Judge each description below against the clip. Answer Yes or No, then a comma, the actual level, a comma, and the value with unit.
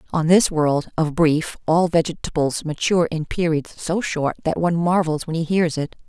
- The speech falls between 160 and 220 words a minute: Yes, average, 190 wpm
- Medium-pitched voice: Yes, medium, 160 Hz